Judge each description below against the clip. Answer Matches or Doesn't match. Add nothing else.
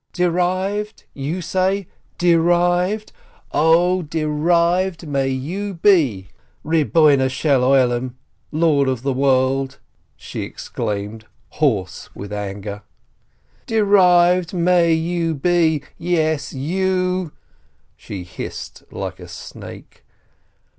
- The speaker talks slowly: Matches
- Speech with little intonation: Doesn't match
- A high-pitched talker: Doesn't match